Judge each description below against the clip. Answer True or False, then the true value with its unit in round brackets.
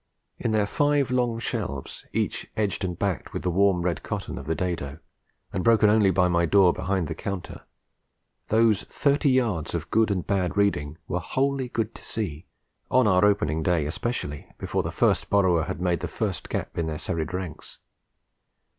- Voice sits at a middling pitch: False (95 Hz)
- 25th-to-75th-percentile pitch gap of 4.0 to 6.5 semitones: True (4.5 semitones)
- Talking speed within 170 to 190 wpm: True (180 wpm)